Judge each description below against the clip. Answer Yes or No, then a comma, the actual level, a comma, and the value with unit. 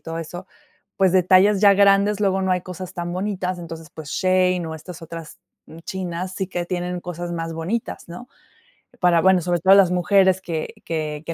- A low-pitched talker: No, medium, 180 Hz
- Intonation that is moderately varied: No, narrow, 2.0 semitones